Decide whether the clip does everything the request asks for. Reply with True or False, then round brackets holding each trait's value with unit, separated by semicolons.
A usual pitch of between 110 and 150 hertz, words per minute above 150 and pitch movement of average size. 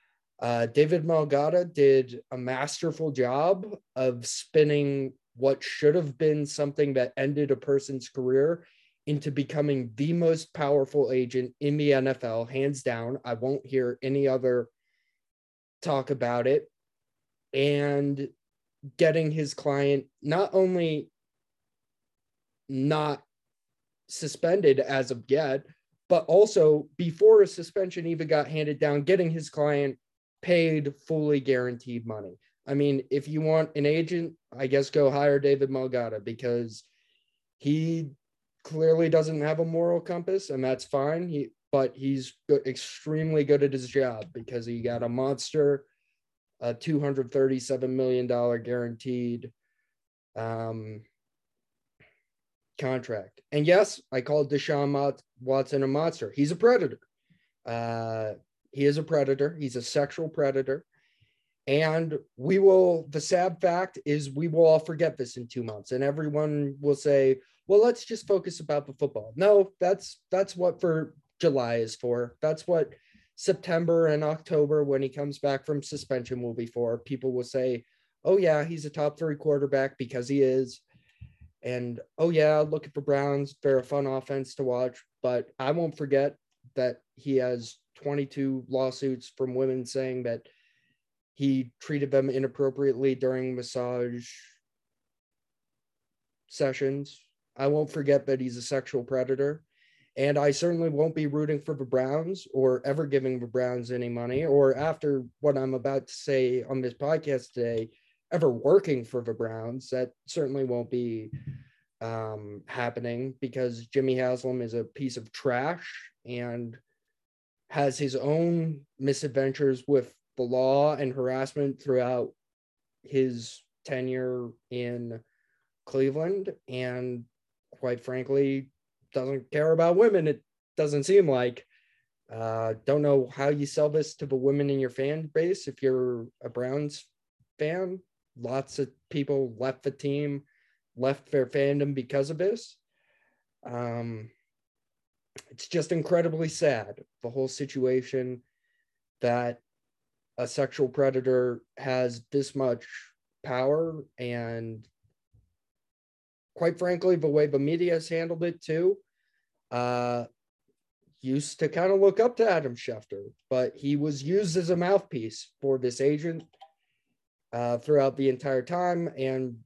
False (140 Hz; 135 wpm; 3.2 semitones)